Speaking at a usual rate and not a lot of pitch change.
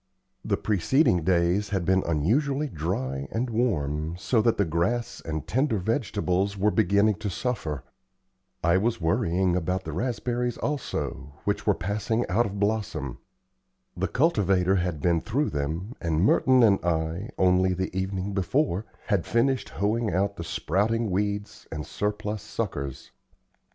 No: average, 145 wpm; average, 4.6 semitones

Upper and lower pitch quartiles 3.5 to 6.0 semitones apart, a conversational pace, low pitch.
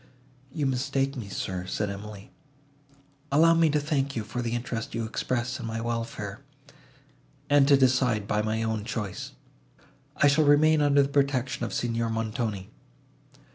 Yes: average, 4.0 semitones; average, 155 wpm; low, 120 Hz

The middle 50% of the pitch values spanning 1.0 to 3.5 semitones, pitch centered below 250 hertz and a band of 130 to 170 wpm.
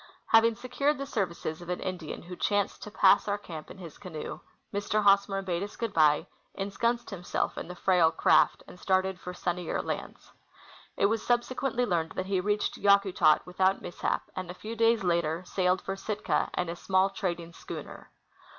No: average, 2.7 semitones; high, 190 Hz; average, 180 wpm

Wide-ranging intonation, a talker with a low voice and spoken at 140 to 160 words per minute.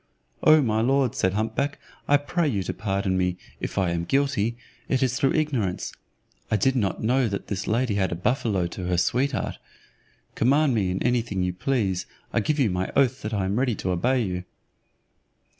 No: wide, 5.9 semitones; low, 110 Hz; average, 195 wpm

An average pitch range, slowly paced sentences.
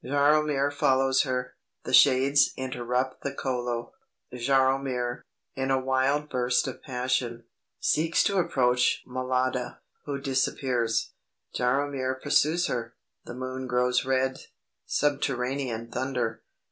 No: narrow, 1.7 semitones; slow, 110 wpm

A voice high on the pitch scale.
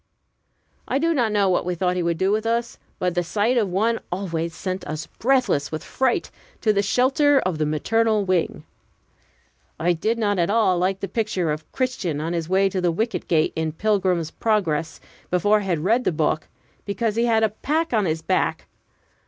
Yes: high, 195 Hz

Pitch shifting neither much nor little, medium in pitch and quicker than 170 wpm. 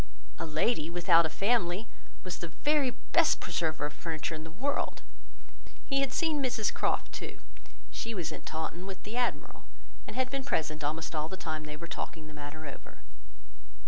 No: wide, 7.1 semitones; medium, 170 Hz; average, 180 wpm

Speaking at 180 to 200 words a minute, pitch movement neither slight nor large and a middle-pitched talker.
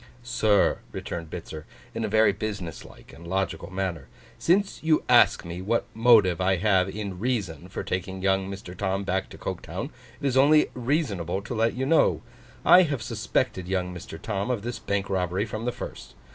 No: average, 185 wpm; average, 4.2 semitones; low, 100 Hz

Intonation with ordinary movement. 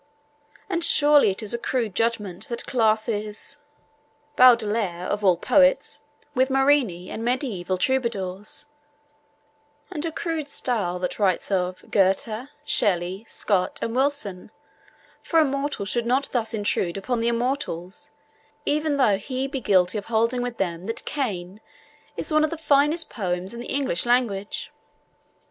No: wide, 5.8 semitones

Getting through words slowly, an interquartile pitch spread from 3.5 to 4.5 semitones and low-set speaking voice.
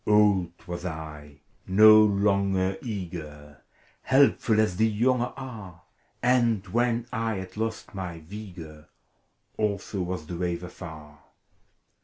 Yes: slow, 115 wpm; average, 4.1 semitones; very low, 95 Hz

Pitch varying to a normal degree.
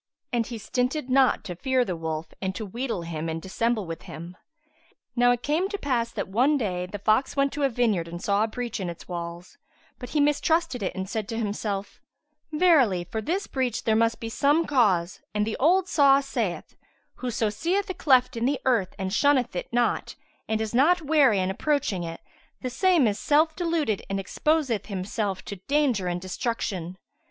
No: wide, 6.5 semitones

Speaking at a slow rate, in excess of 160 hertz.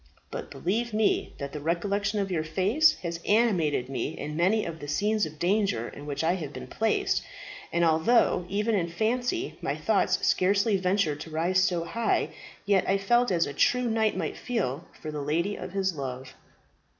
No: average, 185 wpm; medium, 185 Hz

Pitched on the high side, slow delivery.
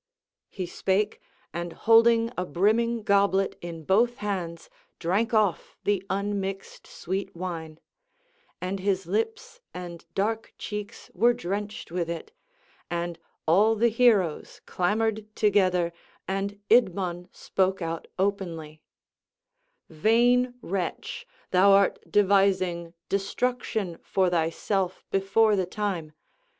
Yes: high, 195 Hz; slow, 110 wpm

